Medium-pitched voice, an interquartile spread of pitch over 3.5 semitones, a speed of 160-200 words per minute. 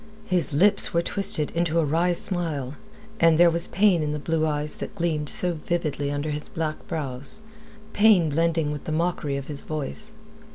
No: medium, 160 Hz; narrow, 2.6 semitones; average, 180 wpm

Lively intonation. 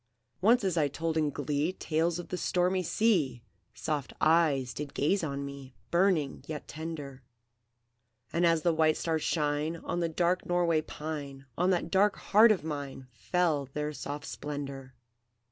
No: average, 3.5 semitones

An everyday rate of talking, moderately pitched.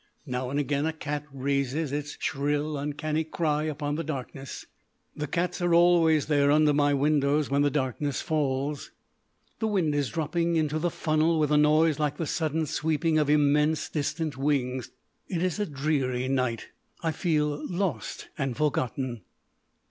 Yes: average, 160 wpm; medium, 150 Hz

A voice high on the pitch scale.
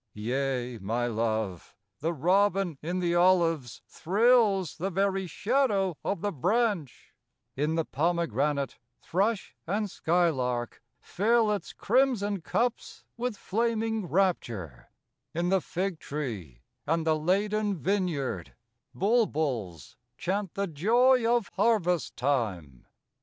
No: medium, 175 Hz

